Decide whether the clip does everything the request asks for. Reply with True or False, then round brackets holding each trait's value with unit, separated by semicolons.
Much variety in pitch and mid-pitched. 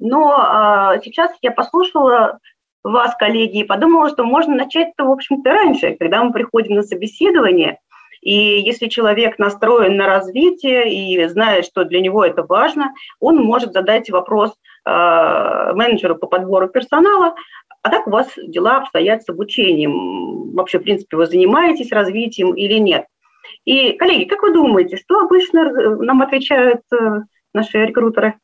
False (6.2 semitones; 235 Hz)